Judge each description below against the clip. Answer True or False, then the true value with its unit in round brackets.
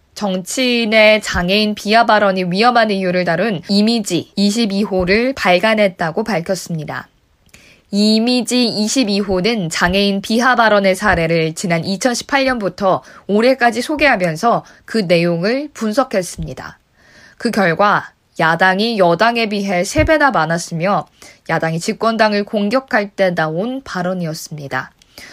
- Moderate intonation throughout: True (4.1 semitones)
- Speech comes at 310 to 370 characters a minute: False (270 characters per minute)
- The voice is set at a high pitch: True (205 Hz)